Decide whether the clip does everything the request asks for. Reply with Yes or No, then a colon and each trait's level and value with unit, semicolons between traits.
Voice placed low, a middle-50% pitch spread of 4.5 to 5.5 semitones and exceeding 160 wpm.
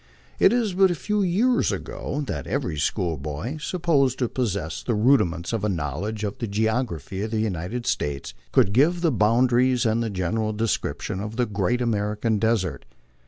Yes: low, 110 Hz; average, 4.9 semitones; average, 180 wpm